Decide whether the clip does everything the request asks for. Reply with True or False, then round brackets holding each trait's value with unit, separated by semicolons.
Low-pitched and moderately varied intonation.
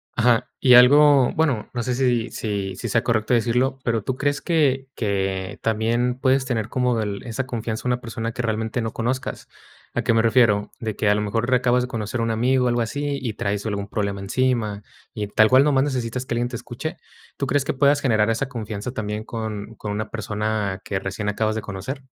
True (115 Hz; 3.1 semitones)